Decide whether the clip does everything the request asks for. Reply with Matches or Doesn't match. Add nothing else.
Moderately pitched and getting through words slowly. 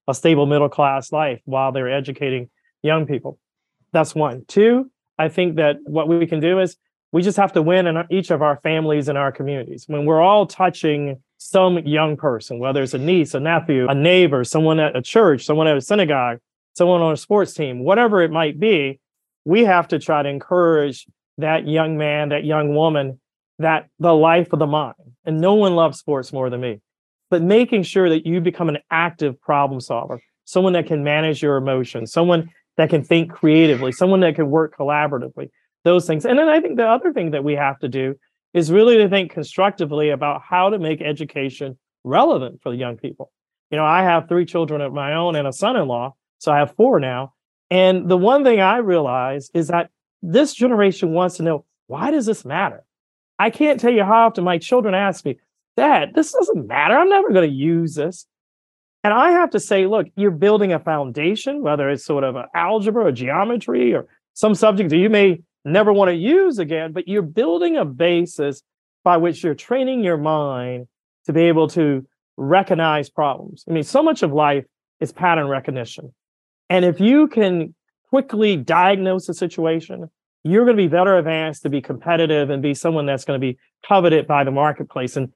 Doesn't match